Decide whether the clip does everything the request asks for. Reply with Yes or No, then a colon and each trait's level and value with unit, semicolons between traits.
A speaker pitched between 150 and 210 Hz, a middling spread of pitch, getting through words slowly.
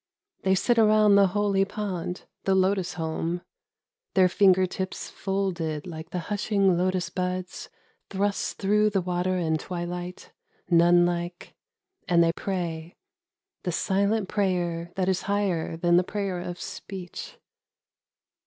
No: medium, 185 Hz; narrow, 2.1 semitones; slow, 130 wpm